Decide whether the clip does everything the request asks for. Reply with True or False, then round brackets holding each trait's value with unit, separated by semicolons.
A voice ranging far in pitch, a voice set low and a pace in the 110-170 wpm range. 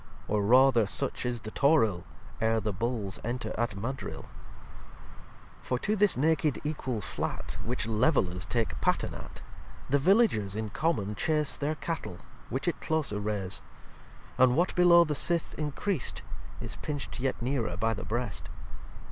True (6.0 semitones; 125 Hz; 150 wpm)